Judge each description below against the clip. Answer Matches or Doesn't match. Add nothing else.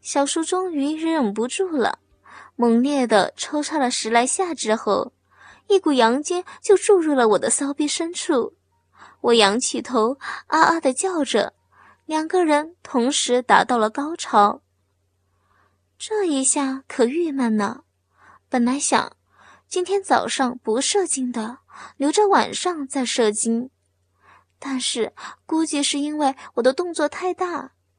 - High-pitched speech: Matches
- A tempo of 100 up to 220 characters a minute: Matches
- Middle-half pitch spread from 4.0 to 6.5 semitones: Matches